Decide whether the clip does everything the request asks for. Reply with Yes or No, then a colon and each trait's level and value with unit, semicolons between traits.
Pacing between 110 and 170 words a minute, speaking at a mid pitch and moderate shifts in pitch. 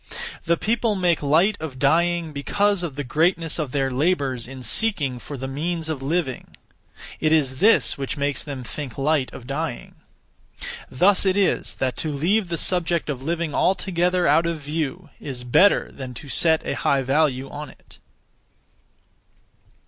Yes: average, 165 wpm; medium, 155 Hz; average, 4.3 semitones